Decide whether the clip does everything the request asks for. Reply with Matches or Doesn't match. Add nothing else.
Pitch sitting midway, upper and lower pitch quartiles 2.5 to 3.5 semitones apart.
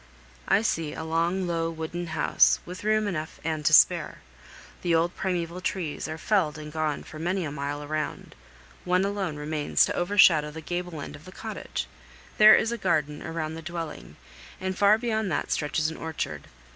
Matches